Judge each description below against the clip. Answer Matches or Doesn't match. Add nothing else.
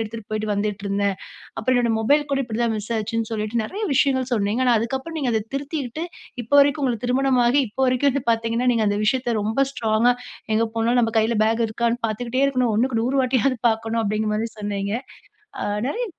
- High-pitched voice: Matches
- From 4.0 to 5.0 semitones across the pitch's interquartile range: Doesn't match